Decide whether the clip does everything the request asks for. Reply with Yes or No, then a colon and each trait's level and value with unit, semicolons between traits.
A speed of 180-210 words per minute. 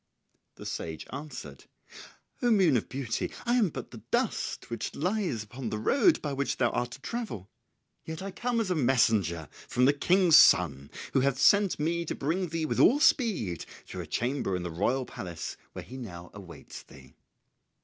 Yes: average, 185 wpm